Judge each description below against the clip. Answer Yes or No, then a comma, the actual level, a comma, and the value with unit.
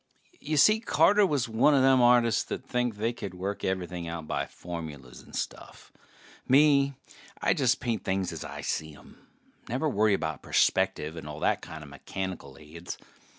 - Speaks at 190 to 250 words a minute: No, average, 165 wpm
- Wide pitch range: Yes, wide, 7.9 semitones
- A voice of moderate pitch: No, low, 100 Hz